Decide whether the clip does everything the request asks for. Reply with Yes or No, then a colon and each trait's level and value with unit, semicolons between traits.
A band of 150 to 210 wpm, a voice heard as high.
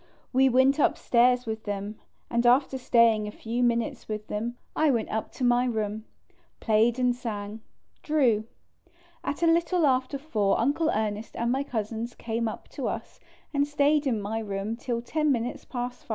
Yes: average, 175 wpm; high, 240 Hz